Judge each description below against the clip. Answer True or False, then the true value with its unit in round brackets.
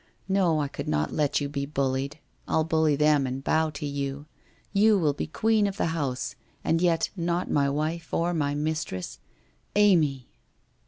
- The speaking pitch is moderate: True (150 Hz)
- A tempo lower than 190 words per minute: True (170 wpm)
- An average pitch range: True (3.2 semitones)